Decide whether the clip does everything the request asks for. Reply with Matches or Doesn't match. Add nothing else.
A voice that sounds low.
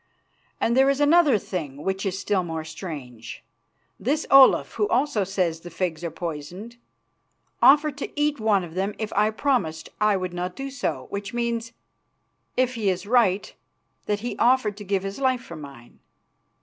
Doesn't match